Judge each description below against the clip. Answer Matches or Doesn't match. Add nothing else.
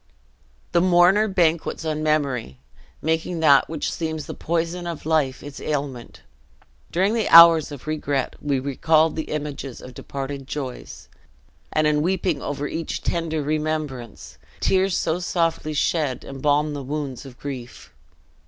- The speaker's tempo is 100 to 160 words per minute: Matches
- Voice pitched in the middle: Matches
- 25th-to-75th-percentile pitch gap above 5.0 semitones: Doesn't match